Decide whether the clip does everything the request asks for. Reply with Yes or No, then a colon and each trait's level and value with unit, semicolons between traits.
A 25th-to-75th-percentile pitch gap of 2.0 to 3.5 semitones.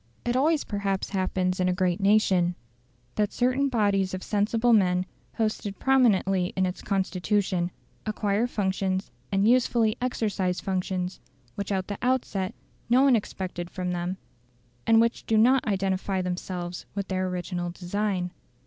Yes: average, 3.1 semitones